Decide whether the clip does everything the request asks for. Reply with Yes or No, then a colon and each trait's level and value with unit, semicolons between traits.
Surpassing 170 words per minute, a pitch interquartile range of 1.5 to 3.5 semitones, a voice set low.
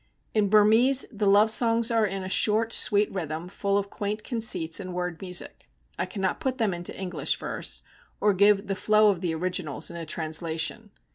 No: average, 190 wpm; average, 3.2 semitones; high, 200 Hz